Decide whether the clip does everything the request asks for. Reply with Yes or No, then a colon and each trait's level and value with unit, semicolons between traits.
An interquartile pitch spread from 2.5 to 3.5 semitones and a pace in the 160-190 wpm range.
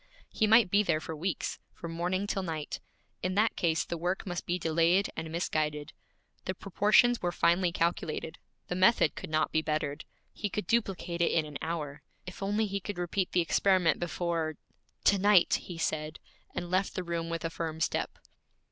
Yes: average, 3.0 semitones; average, 185 wpm